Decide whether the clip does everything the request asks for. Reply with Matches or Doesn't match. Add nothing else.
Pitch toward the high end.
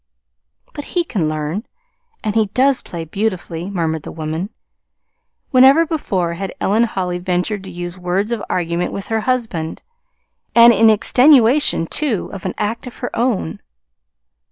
Matches